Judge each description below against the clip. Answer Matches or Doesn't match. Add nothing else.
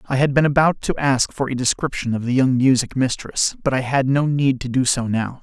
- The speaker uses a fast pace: Matches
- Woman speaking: Doesn't match